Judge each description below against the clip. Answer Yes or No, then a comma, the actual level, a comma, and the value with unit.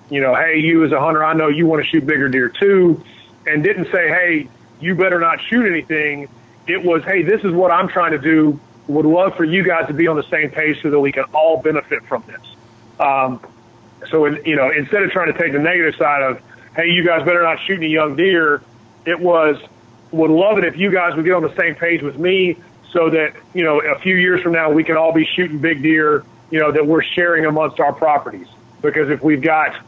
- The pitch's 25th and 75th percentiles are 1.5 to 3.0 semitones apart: Yes, average, 2.7 semitones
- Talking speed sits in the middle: No, fast, 245 wpm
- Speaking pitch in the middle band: Yes, medium, 155 Hz